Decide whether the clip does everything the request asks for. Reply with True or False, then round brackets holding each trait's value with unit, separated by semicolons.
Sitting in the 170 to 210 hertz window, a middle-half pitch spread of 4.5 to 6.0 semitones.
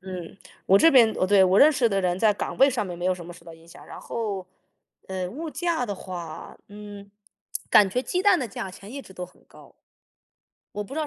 True (200 Hz; 5.3 semitones)